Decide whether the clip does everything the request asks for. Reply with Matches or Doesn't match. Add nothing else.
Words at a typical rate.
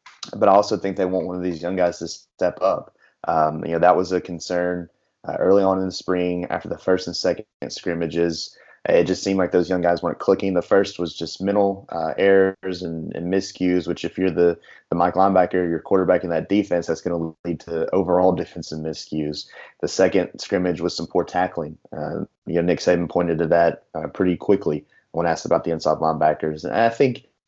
Doesn't match